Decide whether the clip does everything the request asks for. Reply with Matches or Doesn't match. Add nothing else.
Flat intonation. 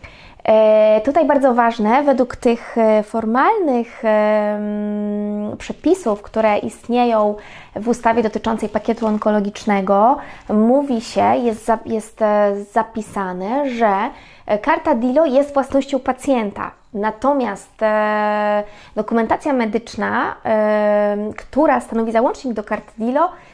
Doesn't match